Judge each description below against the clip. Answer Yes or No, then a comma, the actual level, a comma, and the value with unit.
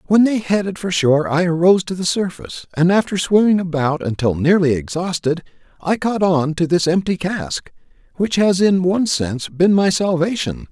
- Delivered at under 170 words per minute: No, average, 175 wpm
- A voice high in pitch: No, medium, 175 Hz